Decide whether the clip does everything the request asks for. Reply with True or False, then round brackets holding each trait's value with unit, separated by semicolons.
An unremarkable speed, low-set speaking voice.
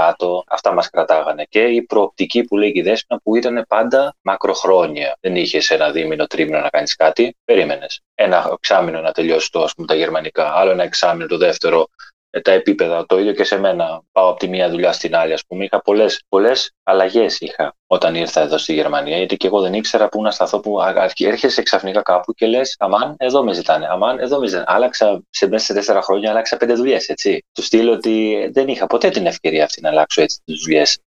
False (205 wpm; 110 Hz)